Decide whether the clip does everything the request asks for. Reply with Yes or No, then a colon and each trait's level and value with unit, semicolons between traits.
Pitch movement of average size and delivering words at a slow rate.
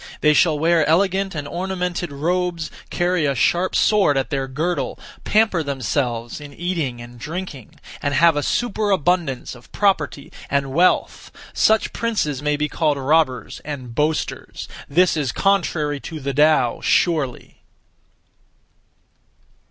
Yes: average, 4.4 semitones; slow, 130 wpm